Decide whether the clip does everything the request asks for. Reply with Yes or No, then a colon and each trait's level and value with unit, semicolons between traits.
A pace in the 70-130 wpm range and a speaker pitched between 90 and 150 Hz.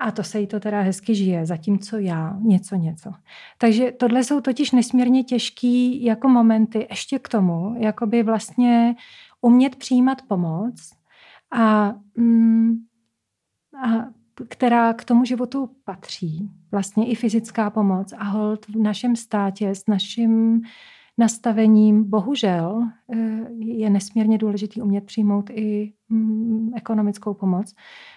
No: average, 120 wpm; high, 225 Hz